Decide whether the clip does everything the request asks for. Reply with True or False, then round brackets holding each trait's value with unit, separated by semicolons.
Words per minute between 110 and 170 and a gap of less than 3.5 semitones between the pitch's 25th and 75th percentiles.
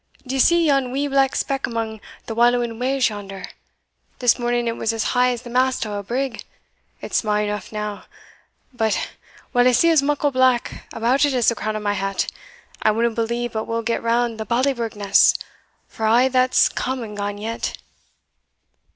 False (185 wpm; 2.8 semitones)